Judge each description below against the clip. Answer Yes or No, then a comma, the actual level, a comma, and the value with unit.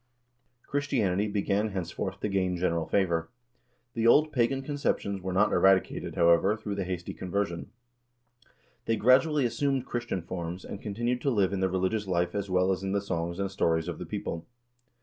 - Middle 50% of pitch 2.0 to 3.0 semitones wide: No, average, 3.8 semitones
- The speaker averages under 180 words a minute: Yes, average, 170 wpm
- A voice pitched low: Yes, low, 100 Hz